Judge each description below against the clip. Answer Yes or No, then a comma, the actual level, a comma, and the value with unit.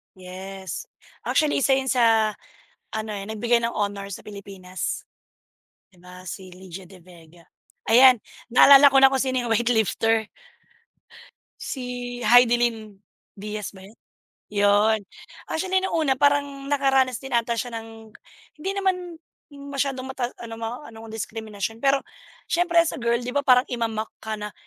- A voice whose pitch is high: Yes, high, 230 Hz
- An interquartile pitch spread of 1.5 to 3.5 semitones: No, average, 4.3 semitones